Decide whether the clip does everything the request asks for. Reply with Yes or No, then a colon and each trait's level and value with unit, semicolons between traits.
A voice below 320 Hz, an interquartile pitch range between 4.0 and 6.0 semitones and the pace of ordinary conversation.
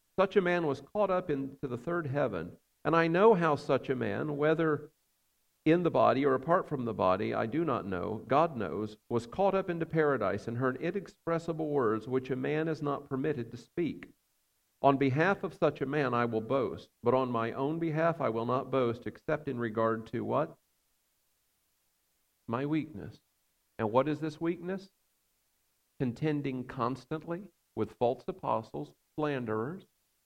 Yes: medium, 140 Hz; wide, 5.4 semitones; average, 170 wpm